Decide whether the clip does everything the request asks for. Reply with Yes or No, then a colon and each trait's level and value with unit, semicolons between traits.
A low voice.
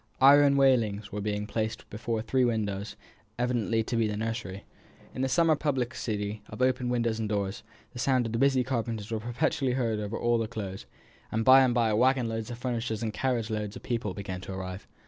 Yes: low, 115 Hz